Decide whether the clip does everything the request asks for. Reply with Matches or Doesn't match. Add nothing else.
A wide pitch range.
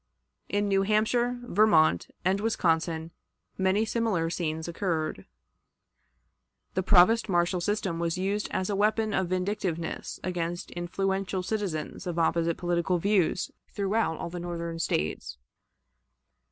Doesn't match